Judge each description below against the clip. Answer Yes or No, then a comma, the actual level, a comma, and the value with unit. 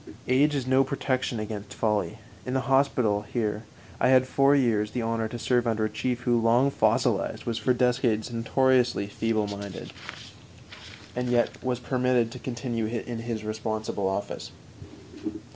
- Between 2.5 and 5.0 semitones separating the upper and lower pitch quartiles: Yes, average, 2.8 semitones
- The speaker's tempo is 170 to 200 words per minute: No, average, 150 wpm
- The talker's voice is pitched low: Yes, low, 120 Hz